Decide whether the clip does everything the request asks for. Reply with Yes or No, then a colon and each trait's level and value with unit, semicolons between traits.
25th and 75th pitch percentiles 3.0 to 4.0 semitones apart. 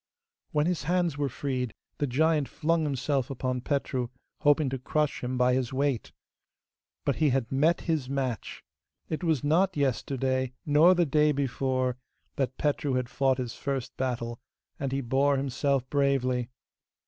No: narrow, 2.5 semitones